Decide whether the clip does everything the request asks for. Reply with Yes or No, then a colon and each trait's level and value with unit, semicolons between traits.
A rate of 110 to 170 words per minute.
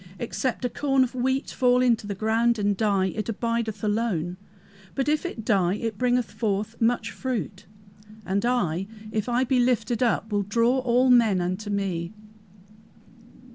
Yes: average, 160 wpm